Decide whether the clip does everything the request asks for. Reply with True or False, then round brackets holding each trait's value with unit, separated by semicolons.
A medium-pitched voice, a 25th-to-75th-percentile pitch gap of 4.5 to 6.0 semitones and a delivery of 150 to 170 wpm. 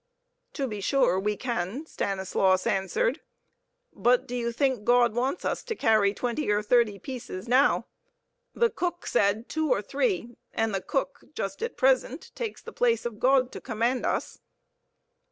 False (240 Hz; 5.0 semitones; 160 wpm)